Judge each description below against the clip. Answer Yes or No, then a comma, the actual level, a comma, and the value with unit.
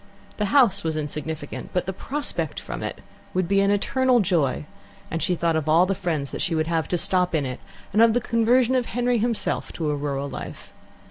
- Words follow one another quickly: Yes, fast, 210 wpm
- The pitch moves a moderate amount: No, wide, 6.4 semitones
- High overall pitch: No, medium, 180 Hz